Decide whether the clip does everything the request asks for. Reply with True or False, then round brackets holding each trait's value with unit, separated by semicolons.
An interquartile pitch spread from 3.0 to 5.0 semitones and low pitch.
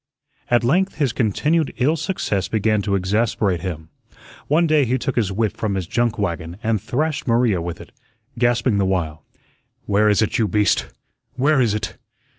True (4.7 semitones; 110 Hz)